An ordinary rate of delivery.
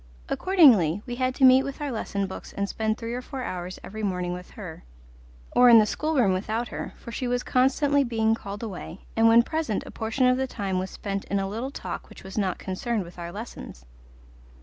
No: fast, 215 wpm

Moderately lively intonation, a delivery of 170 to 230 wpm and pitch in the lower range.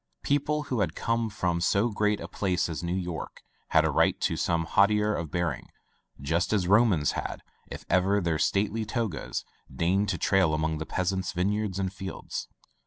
Yes: average, 3.6 semitones; average, 175 wpm; very low, 95 Hz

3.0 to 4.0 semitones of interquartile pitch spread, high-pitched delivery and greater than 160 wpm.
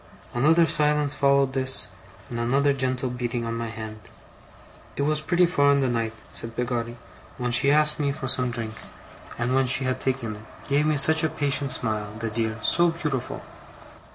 No: average, 3.6 semitones; low, 130 Hz; average, 180 wpm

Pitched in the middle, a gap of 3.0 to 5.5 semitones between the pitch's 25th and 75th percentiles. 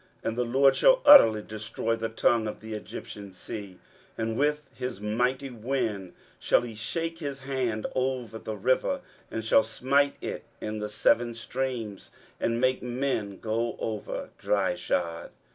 No: low, 115 Hz; average, 3.5 semitones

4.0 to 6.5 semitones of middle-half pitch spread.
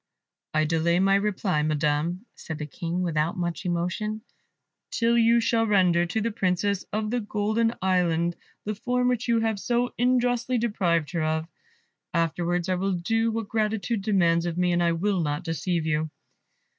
Yes: average, 4.7 semitones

